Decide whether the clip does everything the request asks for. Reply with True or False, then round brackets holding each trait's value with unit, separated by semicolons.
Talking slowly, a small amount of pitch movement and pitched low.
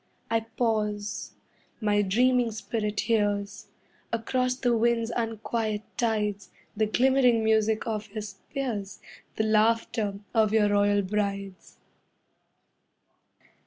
False (100 wpm; 2.0 semitones; 215 Hz)